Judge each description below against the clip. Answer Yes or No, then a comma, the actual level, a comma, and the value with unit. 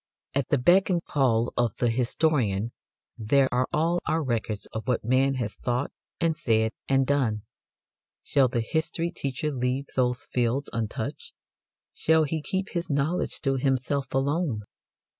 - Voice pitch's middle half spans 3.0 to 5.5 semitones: Yes, average, 4.1 semitones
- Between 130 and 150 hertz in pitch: Yes, low, 135 Hz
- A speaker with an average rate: Yes, average, 150 wpm